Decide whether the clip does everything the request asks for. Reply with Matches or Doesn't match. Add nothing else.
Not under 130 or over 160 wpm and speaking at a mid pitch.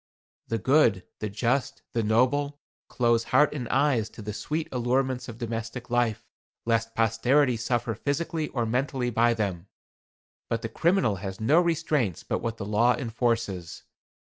Doesn't match